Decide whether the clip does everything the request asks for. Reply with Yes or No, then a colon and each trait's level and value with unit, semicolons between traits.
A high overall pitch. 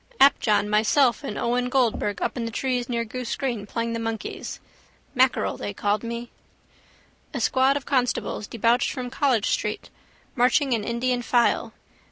Yes: high, 240 Hz